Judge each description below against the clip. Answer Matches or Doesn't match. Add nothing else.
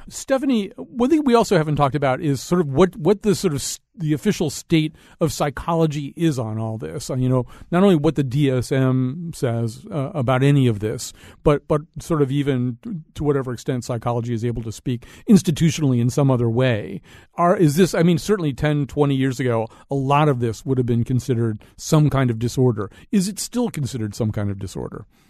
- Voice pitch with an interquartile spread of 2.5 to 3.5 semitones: Doesn't match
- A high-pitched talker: Doesn't match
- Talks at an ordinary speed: Doesn't match